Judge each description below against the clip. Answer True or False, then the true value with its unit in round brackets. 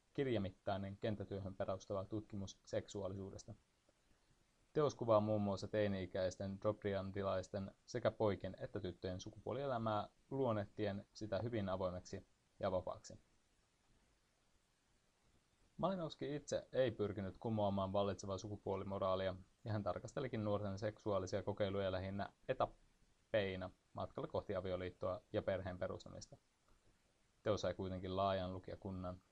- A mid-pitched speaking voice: False (100 Hz)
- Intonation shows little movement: True (2.0 semitones)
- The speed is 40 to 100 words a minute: True (95 wpm)